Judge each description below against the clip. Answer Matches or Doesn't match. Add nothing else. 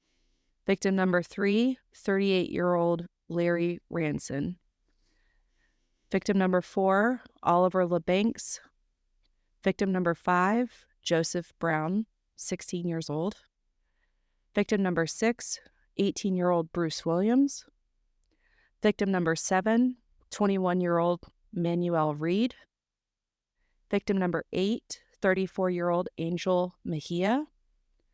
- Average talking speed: Doesn't match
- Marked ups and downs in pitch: Doesn't match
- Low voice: Doesn't match